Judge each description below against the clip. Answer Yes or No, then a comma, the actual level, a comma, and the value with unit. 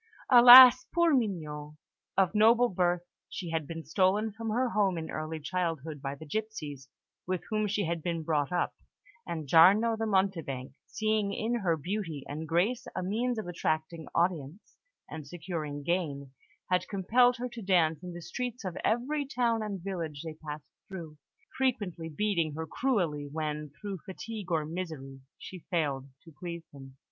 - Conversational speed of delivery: Yes, average, 165 wpm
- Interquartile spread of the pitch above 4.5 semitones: Yes, wide, 5.4 semitones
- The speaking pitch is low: No, medium, 175 Hz